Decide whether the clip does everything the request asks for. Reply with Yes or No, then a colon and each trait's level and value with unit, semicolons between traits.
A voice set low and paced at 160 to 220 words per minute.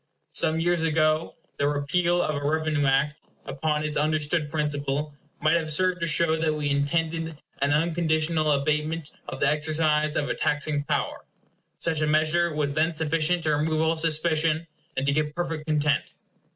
No: medium, 155 Hz; average, 165 wpm